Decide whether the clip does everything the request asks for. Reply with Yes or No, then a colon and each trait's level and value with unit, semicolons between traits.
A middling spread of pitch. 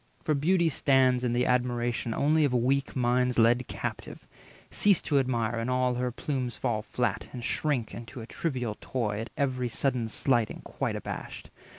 No: narrow, 2.3 semitones